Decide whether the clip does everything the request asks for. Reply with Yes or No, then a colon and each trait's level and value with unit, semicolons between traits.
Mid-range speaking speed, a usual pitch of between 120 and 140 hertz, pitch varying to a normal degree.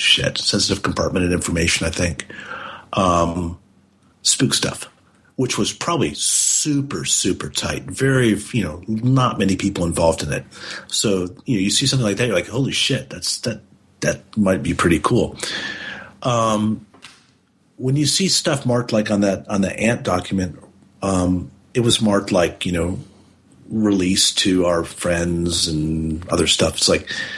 No: average, 160 wpm; very low, 95 Hz; average, 4.4 semitones